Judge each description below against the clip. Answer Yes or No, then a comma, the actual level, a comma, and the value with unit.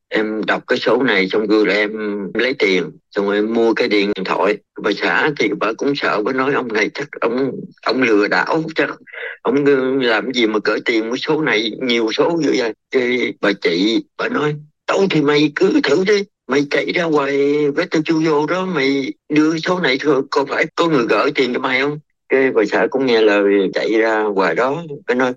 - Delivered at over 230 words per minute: No, average, 215 wpm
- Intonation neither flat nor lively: No, wide, 5.8 semitones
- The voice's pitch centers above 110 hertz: Yes, medium, 140 Hz